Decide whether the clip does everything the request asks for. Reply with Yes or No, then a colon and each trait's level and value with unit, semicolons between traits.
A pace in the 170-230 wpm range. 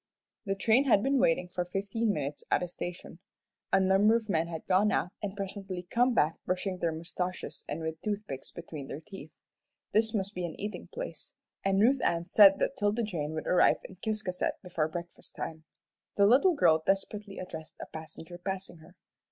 Yes: average, 185 wpm